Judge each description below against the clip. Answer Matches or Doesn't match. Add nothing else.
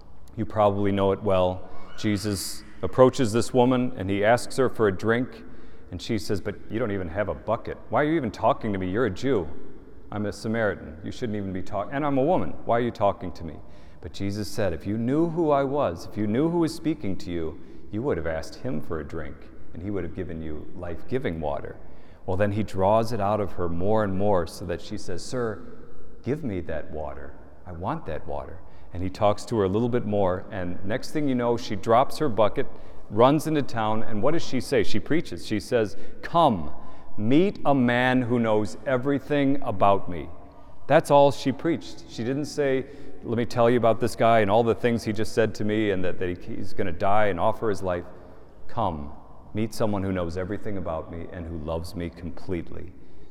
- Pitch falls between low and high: Doesn't match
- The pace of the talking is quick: Matches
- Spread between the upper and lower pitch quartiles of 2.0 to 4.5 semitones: Doesn't match